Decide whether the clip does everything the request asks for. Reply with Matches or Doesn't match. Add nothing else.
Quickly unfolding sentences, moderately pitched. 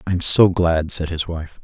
Doesn't match